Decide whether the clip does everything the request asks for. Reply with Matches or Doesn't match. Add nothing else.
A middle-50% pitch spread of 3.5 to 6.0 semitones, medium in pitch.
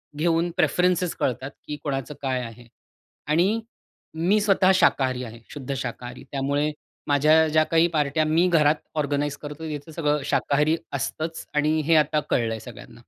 Doesn't match